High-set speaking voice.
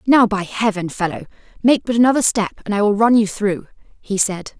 Yes: high, 210 Hz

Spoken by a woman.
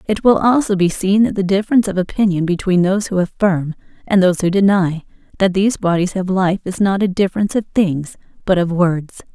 Yes: female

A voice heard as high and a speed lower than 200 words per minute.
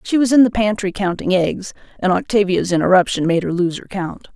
No: high, 195 Hz; fast, 205 wpm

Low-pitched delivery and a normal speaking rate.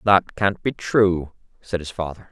Yes: very low, 90 Hz; average, 180 wpm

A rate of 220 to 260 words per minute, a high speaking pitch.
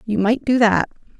No: average, 200 wpm; high, 220 Hz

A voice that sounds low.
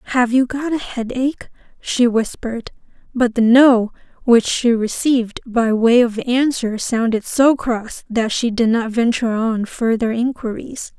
No: high, 235 Hz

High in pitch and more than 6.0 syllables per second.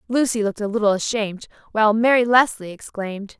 Yes: high, 215 Hz; 6.5 syllables/s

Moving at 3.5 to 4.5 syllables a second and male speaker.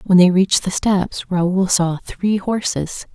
No: 3.7 syllables/s; female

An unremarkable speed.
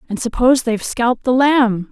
Yes: average, 190 wpm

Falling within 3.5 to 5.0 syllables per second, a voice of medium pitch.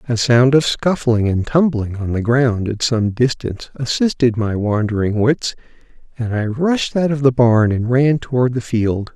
No: 4.5 syllables/s; low, 120 Hz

